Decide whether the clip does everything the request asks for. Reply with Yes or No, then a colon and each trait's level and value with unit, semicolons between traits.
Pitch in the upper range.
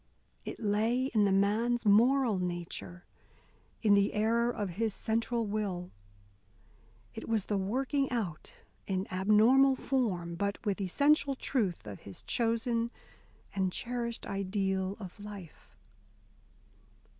Yes: high, 210 Hz